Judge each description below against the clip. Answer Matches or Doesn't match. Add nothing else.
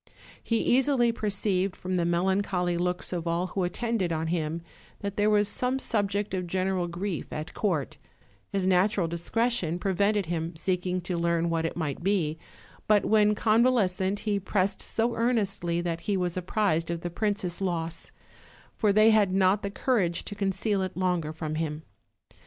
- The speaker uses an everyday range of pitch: Matches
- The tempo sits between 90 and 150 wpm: Doesn't match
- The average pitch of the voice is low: Doesn't match